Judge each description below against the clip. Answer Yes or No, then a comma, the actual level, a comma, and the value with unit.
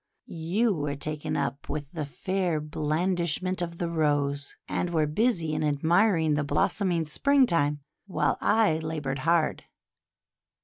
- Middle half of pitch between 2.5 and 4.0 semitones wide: Yes, average, 3.3 semitones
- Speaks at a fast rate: No, slow, 135 wpm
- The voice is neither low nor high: Yes, medium, 160 Hz